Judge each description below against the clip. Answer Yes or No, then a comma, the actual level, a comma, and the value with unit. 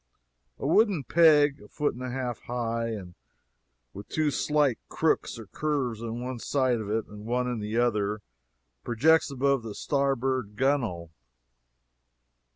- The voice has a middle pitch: No, low, 125 Hz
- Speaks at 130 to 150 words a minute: Yes, average, 145 wpm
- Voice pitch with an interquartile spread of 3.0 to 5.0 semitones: Yes, average, 3.8 semitones